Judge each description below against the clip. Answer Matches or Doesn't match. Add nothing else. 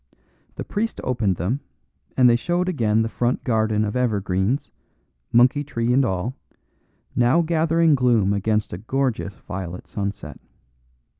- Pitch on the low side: Matches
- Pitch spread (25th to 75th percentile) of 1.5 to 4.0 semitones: Doesn't match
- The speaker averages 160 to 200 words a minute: Doesn't match